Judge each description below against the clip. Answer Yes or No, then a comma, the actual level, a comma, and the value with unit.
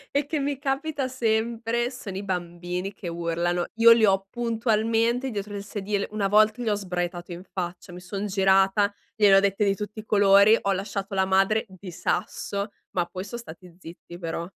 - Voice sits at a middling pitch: No, high, 200 Hz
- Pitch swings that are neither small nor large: Yes, average, 3.2 semitones